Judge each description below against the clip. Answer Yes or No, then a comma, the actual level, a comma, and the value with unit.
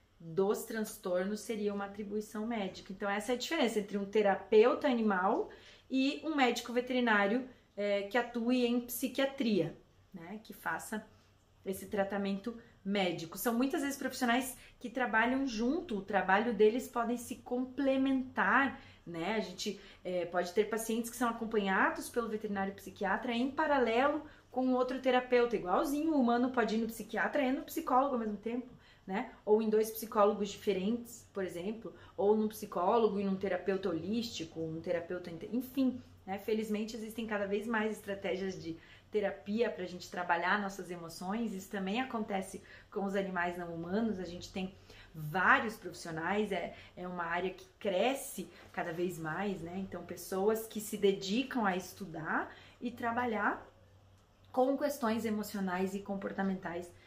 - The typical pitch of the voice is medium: No, high, 210 Hz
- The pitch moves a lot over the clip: No, average, 4.0 semitones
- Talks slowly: No, average, 150 wpm